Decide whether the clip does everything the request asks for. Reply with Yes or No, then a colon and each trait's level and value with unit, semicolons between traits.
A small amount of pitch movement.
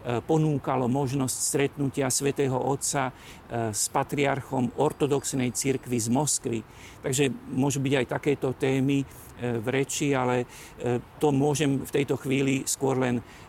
Yes: narrow, 2.2 semitones